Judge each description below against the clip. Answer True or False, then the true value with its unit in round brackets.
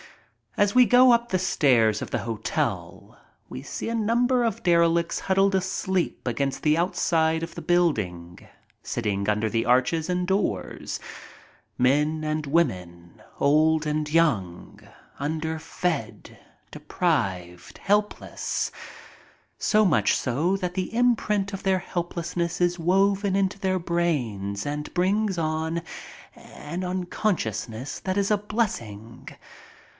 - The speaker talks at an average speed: False (120 wpm)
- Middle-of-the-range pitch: True (170 Hz)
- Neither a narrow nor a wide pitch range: False (6.6 semitones)